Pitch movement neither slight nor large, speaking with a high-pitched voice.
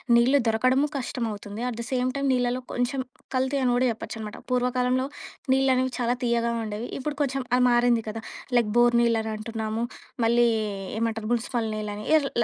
No: narrow, 2.3 semitones; high, 240 Hz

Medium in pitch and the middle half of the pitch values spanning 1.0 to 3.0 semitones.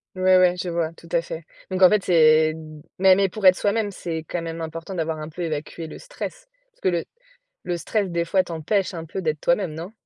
Yes: medium, 170 Hz; narrow, 2.6 semitones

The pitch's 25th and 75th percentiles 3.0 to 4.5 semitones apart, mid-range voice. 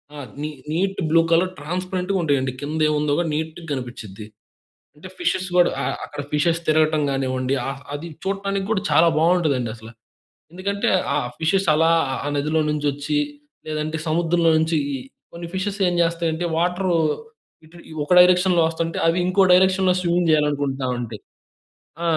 Yes: average, 3.4 semitones; medium, 165 Hz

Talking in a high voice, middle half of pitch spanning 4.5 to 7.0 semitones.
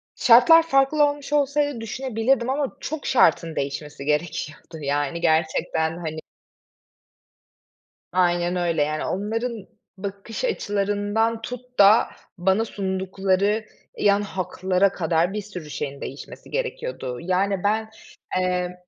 Yes: high, 195 Hz; average, 5.3 semitones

